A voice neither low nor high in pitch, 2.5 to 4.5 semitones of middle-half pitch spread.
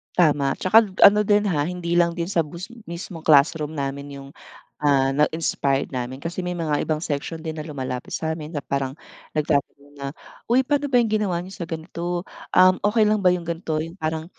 Yes: medium, 160 Hz; average, 3.8 semitones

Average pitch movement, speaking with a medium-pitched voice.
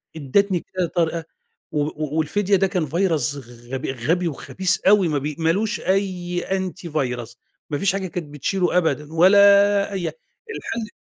Yes: average, 4.2 semitones; medium, 175 Hz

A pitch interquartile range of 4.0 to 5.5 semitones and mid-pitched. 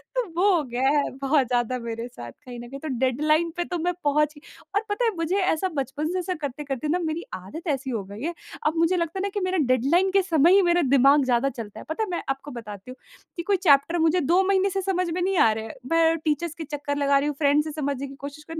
No: average, 4.5 semitones; very high, 300 Hz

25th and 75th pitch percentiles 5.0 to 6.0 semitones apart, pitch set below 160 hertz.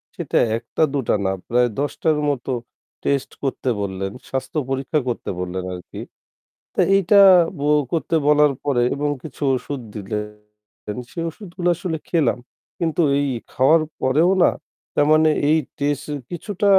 Yes: average, 5.3 semitones; medium, 140 Hz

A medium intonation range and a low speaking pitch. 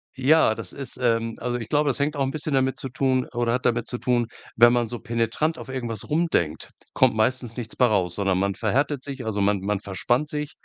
Yes: average, 3.4 semitones; low, 120 Hz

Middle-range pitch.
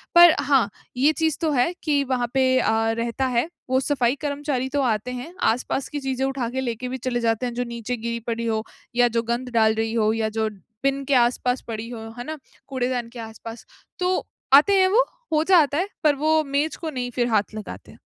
No: very high, 255 Hz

